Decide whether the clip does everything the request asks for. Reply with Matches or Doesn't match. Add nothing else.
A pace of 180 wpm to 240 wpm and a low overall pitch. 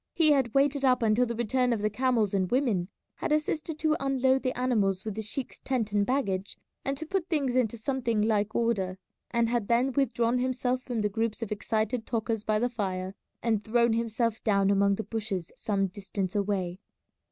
Doesn't match